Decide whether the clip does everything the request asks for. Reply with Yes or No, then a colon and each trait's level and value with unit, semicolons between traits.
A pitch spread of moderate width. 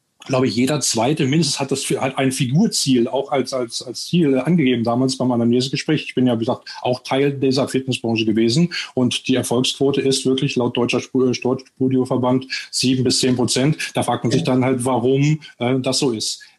No: narrow, 1.8 semitones